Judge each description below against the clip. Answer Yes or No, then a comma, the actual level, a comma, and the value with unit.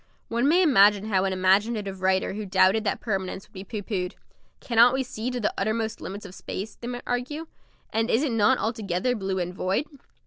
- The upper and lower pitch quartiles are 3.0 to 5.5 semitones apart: Yes, average, 3.7 semitones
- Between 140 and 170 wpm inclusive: No, fast, 205 wpm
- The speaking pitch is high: Yes, high, 210 Hz